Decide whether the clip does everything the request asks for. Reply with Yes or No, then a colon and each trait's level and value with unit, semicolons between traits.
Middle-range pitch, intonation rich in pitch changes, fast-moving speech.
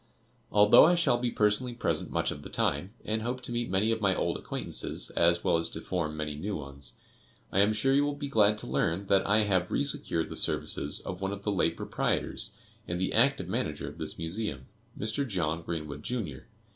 No: low, 100 Hz; wide, 5.7 semitones; fast, 215 wpm